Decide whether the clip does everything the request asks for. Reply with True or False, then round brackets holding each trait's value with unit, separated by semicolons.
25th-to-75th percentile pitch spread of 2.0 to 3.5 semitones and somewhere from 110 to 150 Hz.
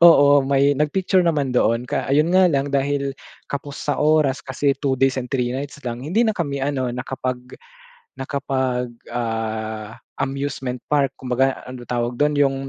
True (2.4 semitones; 135 Hz)